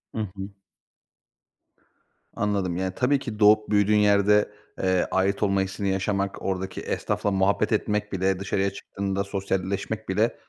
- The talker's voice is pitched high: No, low, 100 Hz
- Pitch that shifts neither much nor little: No, narrow, 1.5 semitones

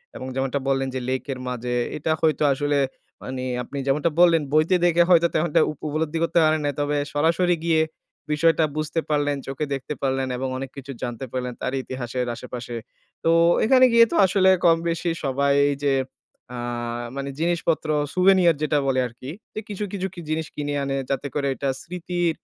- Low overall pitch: No, medium, 150 Hz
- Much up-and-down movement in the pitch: No, average, 3.8 semitones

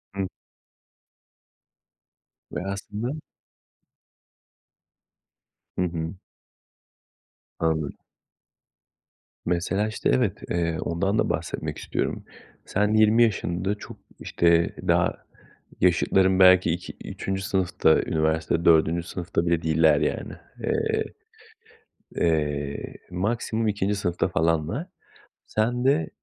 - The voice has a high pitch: No, very low, 90 Hz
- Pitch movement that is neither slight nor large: Yes, average, 4.0 semitones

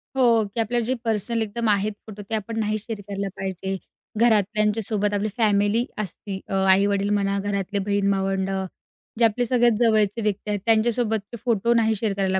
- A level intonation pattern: Yes, narrow, 2.2 semitones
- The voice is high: Yes, high, 210 Hz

